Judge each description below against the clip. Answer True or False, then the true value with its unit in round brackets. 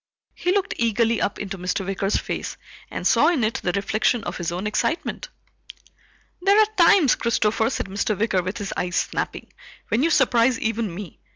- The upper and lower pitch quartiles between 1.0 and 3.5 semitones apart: False (5.1 semitones)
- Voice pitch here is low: False (220 Hz)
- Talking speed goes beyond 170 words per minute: True (180 wpm)